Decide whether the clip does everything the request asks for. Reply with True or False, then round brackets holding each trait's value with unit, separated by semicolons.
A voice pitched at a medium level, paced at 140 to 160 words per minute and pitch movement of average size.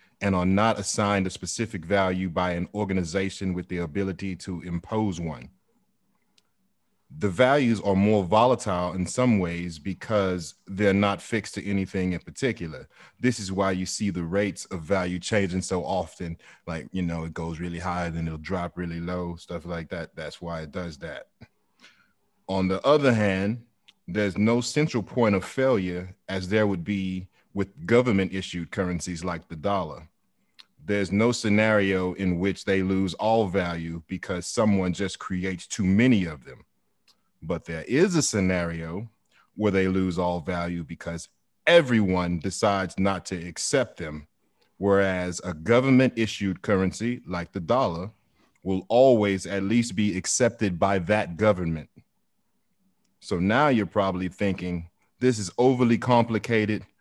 False (95 Hz; 155 wpm; 3.0 semitones)